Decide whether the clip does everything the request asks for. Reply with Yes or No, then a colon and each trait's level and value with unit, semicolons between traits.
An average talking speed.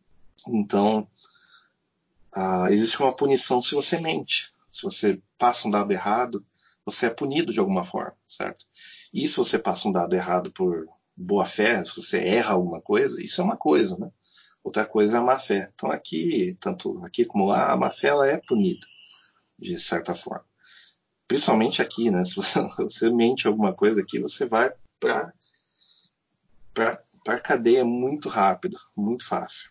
Yes: average, 160 wpm